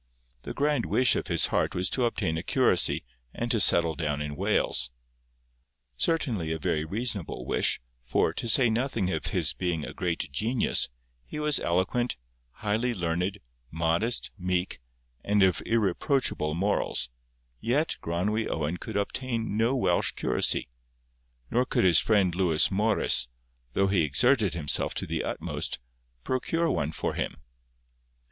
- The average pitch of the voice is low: Yes, very low, 95 Hz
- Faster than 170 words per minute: No, average, 145 wpm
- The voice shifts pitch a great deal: Yes, wide, 6.2 semitones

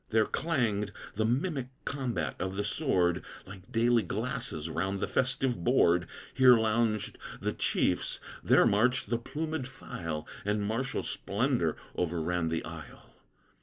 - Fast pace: No, slow, 135 wpm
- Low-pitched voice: Yes, low, 110 Hz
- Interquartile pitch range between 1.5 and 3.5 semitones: No, average, 5.3 semitones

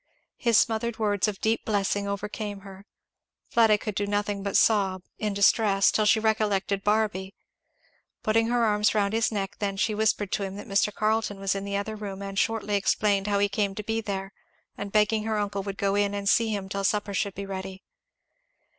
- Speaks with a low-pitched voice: No, high, 205 Hz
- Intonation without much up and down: Yes, narrow, 1.5 semitones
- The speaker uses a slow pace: No, average, 200 wpm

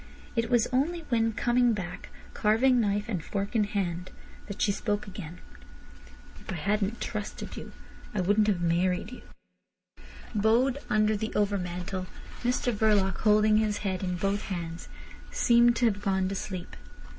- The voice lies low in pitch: No, high, 205 Hz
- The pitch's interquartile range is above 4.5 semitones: No, average, 3.1 semitones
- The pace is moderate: Yes, average, 155 wpm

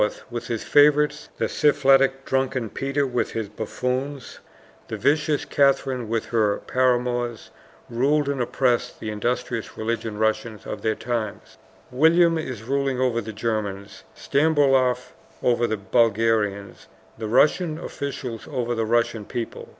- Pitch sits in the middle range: No, low, 120 Hz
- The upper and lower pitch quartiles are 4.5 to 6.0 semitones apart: No, average, 3.5 semitones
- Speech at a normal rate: No, slow, 130 wpm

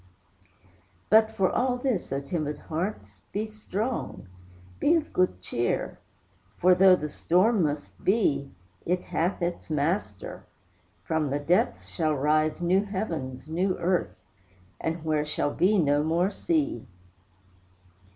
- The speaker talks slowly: Yes, slow, 125 wpm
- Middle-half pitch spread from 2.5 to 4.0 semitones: No, average, 5.3 semitones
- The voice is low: No, medium, 175 Hz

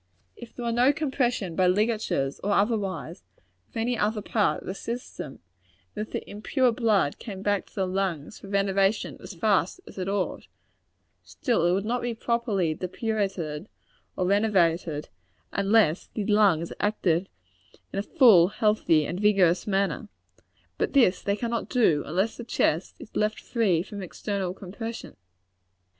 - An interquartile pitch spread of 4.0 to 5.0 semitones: No, average, 3.6 semitones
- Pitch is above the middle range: Yes, high, 200 Hz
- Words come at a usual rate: Yes, average, 155 wpm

